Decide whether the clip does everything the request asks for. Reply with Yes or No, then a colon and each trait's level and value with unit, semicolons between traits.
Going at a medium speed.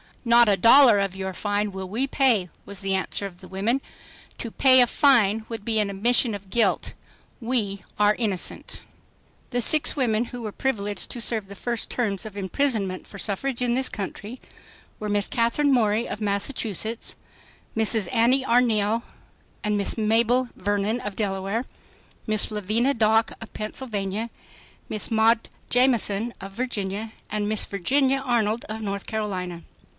Yes: average, 155 wpm